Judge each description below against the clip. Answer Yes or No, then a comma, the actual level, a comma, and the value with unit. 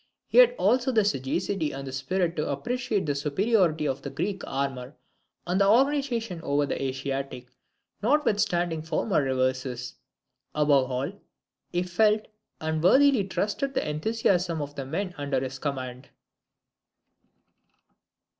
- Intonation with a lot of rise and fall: Yes, wide, 7.1 semitones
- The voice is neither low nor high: Yes, medium, 160 Hz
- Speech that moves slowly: Yes, slow, 125 wpm